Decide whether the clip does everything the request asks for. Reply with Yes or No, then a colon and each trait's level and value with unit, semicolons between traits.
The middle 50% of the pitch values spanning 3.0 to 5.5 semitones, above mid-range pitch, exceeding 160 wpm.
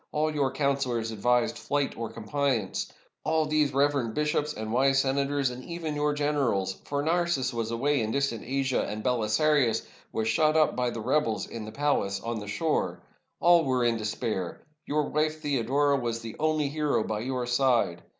No: average, 4.3 semitones; low, 135 Hz; average, 175 wpm